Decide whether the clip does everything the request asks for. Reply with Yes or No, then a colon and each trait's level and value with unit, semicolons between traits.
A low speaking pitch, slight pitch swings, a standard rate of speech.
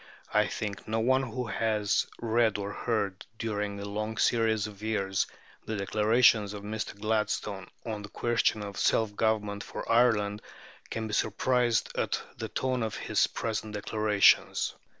Yes: low, 110 Hz; narrow, 1.6 semitones; average, 150 wpm